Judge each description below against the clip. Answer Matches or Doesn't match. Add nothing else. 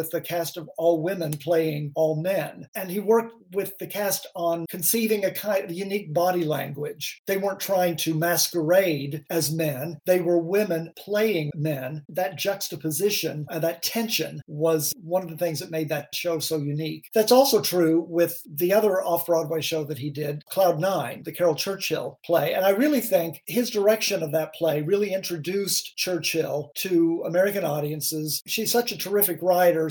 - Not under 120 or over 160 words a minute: Doesn't match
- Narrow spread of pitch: Doesn't match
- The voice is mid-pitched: Matches